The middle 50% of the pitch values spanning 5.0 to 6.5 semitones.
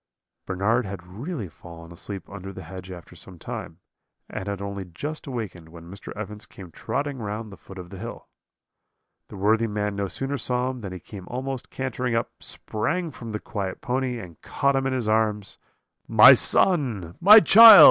Yes: average, 5.3 semitones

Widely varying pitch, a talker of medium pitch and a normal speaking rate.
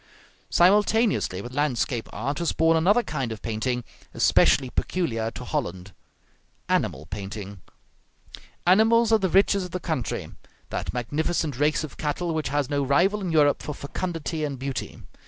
Yes: wide, 6.2 semitones; medium, 145 Hz; average, 150 wpm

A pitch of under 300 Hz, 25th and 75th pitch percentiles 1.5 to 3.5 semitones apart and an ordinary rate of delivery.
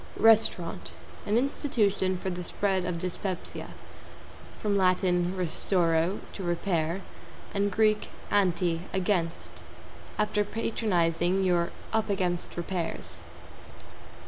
No: medium, 185 Hz; average, 2.9 semitones; slow, 95 wpm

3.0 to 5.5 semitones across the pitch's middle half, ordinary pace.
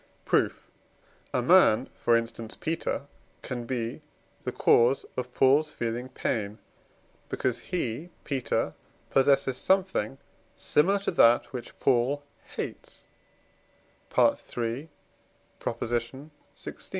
No: average, 3.5 semitones; slow, 95 wpm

